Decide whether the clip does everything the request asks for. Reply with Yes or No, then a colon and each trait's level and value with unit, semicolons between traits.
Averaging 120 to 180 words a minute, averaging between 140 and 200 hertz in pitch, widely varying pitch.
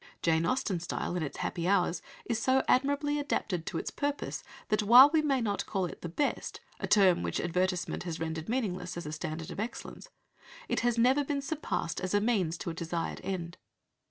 No: average, 200 wpm; high, 190 Hz; wide, 7.1 semitones